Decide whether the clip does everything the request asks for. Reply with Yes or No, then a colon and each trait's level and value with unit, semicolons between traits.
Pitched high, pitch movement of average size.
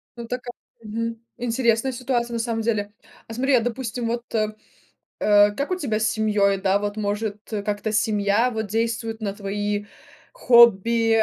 No: high, 225 Hz; narrow, 2.3 semitones